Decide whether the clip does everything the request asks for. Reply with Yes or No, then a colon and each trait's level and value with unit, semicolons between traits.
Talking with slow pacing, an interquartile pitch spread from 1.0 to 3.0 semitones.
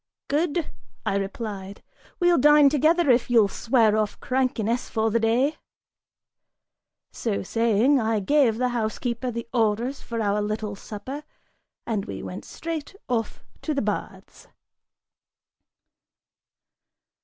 No: slow, 120 wpm; average, 4.3 semitones